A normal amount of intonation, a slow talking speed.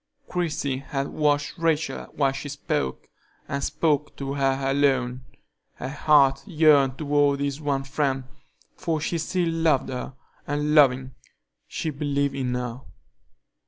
No: narrow, 1.9 semitones; slow, 130 wpm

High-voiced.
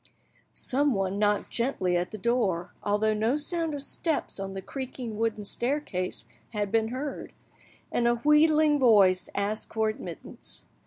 Yes: high, 225 Hz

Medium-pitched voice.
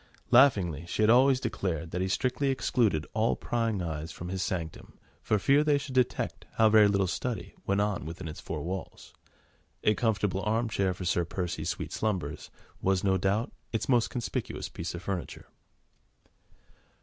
No: low, 100 Hz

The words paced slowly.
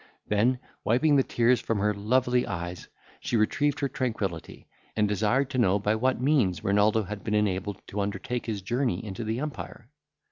No: average, 175 wpm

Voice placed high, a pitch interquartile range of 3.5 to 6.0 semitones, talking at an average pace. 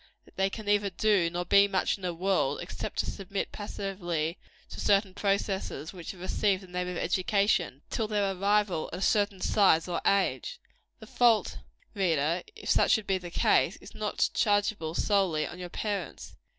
No: high, 195 Hz; narrow, 2.5 semitones; average, 180 wpm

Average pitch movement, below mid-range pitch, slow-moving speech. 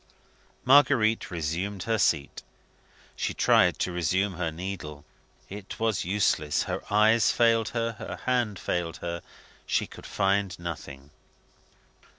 Yes: average, 4.6 semitones; very low, 95 Hz; slow, 125 wpm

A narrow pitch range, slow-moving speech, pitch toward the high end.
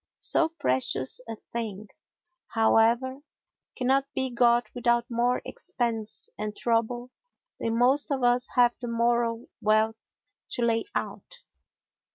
Yes: narrow, 1.7 semitones; slow, 120 wpm; high, 235 Hz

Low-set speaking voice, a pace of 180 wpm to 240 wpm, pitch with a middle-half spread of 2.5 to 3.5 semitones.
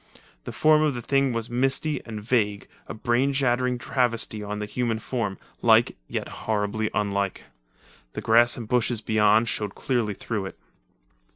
No: low, 115 Hz; average, 160 wpm; average, 2.9 semitones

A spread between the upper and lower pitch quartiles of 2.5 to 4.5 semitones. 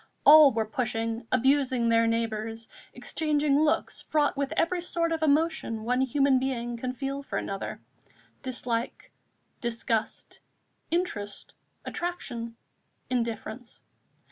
Yes: average, 4.2 semitones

